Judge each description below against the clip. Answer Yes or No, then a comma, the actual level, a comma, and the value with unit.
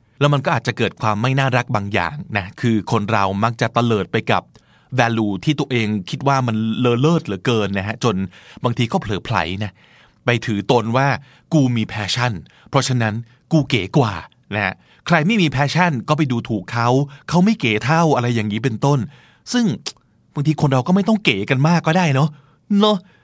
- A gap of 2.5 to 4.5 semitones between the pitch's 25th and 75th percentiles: No, average, 5.1 semitones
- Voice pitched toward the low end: Yes, low, 125 Hz